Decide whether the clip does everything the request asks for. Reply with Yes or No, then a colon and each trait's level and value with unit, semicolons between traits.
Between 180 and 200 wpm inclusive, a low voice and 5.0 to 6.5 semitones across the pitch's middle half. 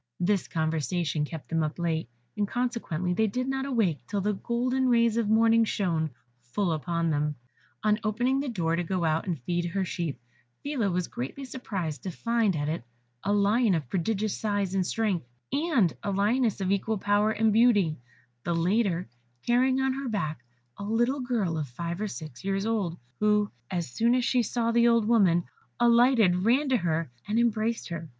No: average, 185 wpm; high, 205 Hz; wide, 5.5 semitones